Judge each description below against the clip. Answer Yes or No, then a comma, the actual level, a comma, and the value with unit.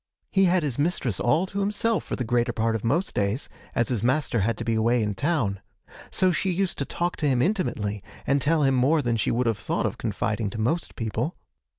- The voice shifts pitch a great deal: Yes, wide, 6.9 semitones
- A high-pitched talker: No, low, 125 Hz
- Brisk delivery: Yes, fast, 230 wpm